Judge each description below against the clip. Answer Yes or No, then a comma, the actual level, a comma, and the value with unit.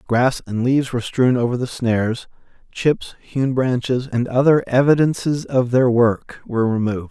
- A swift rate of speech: No, average, 160 wpm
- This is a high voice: No, low, 125 Hz